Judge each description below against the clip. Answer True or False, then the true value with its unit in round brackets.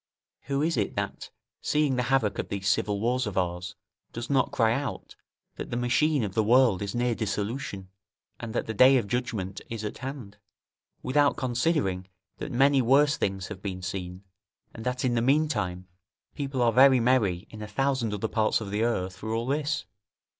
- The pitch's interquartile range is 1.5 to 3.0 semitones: False (4.7 semitones)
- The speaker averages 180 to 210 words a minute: True (190 wpm)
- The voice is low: True (115 Hz)